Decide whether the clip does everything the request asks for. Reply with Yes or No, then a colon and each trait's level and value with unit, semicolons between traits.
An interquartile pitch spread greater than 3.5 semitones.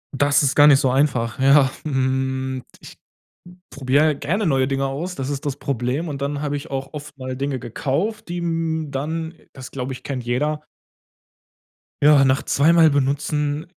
No: narrow, 2.4 semitones